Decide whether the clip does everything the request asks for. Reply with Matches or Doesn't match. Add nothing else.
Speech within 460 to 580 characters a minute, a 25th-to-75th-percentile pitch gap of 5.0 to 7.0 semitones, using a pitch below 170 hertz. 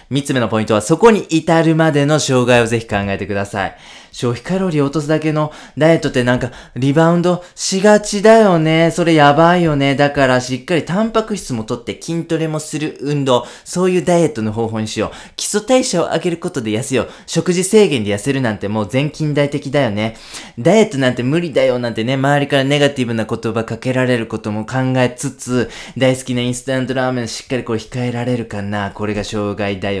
Doesn't match